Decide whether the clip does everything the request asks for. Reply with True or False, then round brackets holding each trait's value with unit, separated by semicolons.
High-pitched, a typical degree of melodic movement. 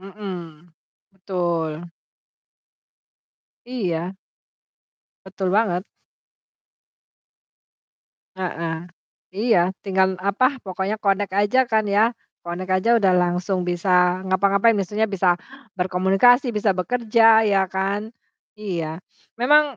True (195 Hz; 3.1 semitones)